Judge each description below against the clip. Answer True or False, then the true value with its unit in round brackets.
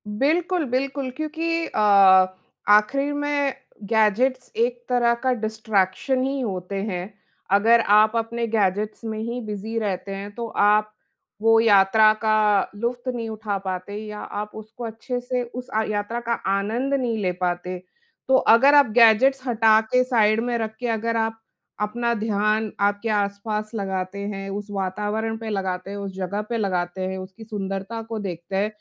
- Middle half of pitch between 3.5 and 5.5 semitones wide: False (2.9 semitones)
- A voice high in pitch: True (220 Hz)